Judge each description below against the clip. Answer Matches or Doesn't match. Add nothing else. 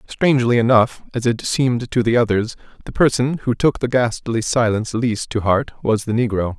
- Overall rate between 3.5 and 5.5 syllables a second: Matches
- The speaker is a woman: Doesn't match